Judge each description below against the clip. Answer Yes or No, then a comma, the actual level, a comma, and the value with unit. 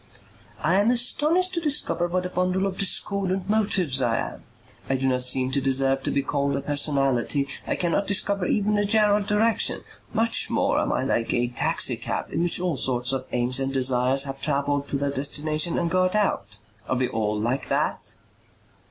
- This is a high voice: No, medium, 145 Hz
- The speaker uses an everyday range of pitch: No, wide, 6.9 semitones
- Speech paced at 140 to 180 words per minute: No, average, 190 wpm